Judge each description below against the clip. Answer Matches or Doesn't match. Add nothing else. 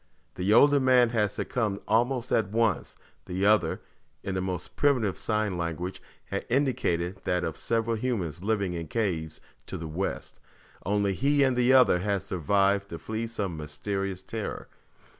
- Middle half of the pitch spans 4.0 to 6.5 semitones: Matches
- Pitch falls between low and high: Doesn't match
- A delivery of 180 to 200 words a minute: Doesn't match